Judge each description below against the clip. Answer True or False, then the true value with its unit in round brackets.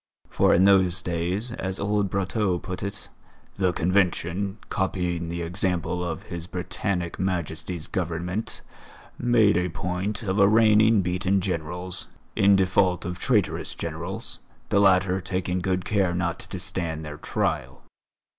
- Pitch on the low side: True (90 Hz)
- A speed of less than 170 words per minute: True (135 wpm)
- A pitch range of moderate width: False (2.1 semitones)